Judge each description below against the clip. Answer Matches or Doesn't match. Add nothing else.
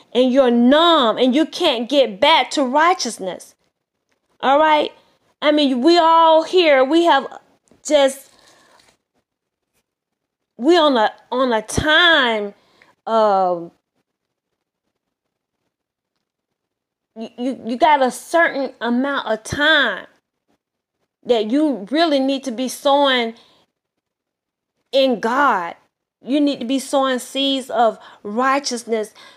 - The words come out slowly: Matches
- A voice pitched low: Doesn't match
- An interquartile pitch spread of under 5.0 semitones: Matches